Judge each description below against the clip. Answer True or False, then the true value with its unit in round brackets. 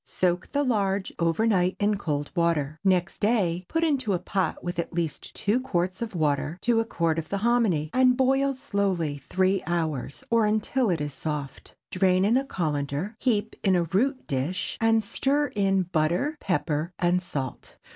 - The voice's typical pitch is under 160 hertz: False (185 Hz)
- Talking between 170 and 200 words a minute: True (180 wpm)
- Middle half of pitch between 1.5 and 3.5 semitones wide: False (5.3 semitones)